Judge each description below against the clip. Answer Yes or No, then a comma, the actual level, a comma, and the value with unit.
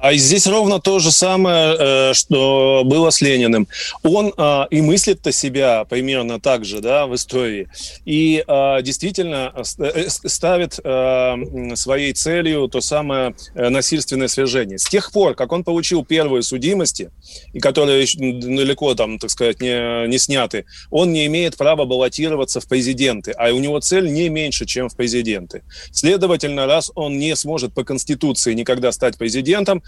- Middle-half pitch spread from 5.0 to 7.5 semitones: No, average, 4.0 semitones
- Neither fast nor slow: Yes, average, 145 wpm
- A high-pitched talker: No, low, 135 Hz